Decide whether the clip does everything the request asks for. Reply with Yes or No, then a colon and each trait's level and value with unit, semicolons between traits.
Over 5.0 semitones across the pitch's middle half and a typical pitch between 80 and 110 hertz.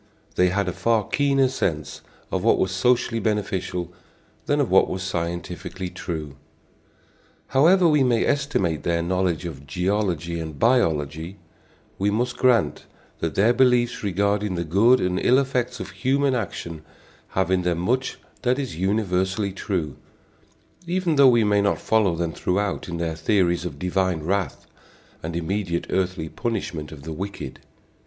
Yes: wide, 5.4 semitones; very low, 95 Hz